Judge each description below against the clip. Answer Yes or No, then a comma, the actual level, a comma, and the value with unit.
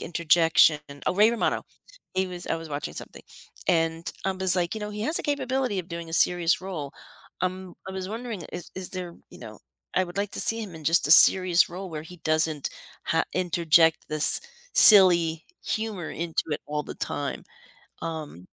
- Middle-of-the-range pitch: Yes, medium, 175 Hz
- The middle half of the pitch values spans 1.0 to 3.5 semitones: Yes, average, 2.7 semitones